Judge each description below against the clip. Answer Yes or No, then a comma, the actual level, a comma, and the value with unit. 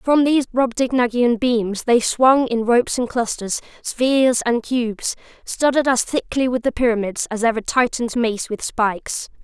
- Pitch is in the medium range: No, high, 240 Hz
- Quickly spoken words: No, average, 155 wpm